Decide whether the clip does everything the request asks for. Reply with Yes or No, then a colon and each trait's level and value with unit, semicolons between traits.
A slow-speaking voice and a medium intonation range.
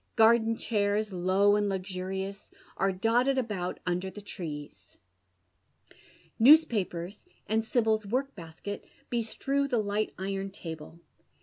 Yes: slow, 110 wpm; average, 3.3 semitones